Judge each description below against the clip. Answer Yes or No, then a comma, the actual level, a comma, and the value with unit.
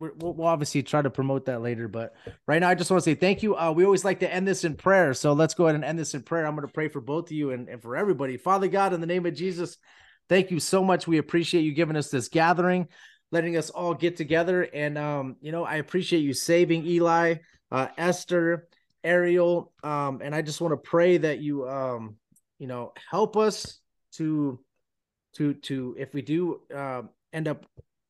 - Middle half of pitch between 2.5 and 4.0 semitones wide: Yes, average, 3.6 semitones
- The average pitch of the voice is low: No, medium, 160 Hz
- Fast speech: Yes, fast, 225 wpm